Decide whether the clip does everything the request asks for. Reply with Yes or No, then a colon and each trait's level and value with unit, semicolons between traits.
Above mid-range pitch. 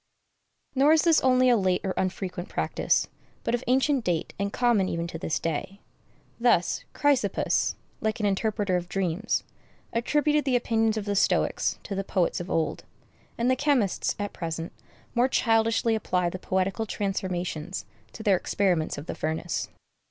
Yes: high, 200 Hz